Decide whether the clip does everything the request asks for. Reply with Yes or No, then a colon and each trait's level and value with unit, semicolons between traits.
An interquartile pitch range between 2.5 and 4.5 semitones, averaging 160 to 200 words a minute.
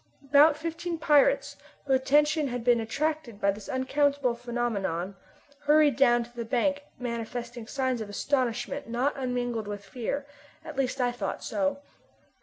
No: average, 3.5 semitones; average, 145 wpm